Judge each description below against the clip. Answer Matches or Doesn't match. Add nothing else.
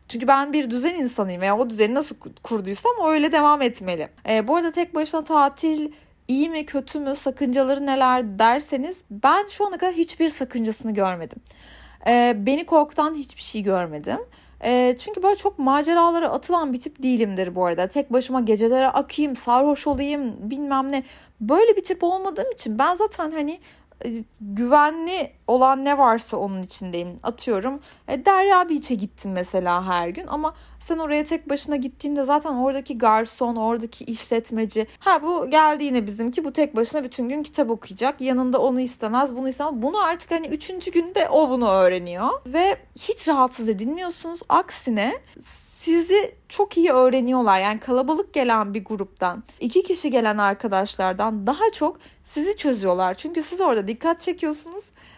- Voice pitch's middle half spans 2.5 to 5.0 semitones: Doesn't match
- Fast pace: Matches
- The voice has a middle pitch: Doesn't match